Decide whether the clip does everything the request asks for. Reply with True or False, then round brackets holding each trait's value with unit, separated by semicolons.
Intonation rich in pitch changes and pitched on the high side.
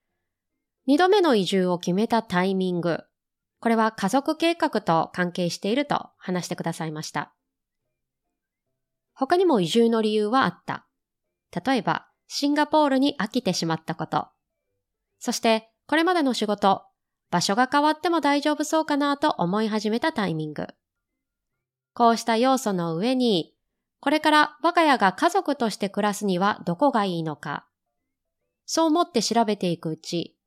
True (8.6 semitones; 215 Hz)